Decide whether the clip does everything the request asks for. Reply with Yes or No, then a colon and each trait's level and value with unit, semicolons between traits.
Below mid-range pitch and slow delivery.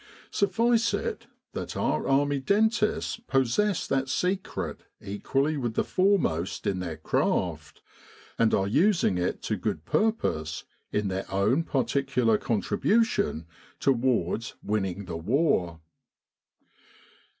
Yes: low, 130 Hz; slow, 115 wpm